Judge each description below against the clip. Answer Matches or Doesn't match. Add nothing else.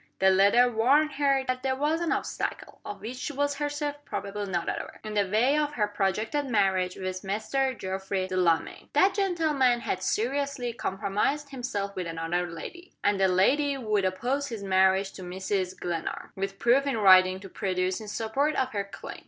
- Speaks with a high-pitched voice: Matches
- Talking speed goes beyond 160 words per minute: Matches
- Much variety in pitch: Matches